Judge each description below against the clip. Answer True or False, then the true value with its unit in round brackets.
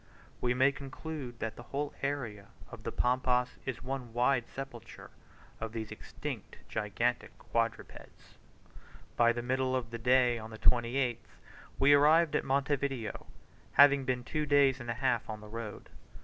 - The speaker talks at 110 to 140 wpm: False (160 wpm)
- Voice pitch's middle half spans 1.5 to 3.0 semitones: True (2.7 semitones)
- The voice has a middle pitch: False (125 Hz)